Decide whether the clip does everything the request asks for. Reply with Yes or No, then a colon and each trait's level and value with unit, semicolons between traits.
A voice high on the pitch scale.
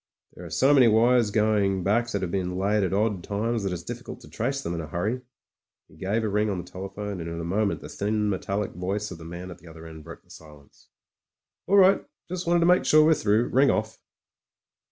No: low, 100 Hz